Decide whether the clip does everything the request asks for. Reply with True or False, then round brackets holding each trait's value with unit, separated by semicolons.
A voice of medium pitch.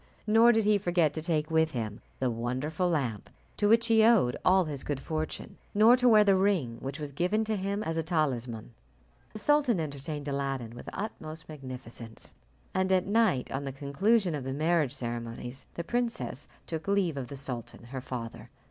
True (155 Hz)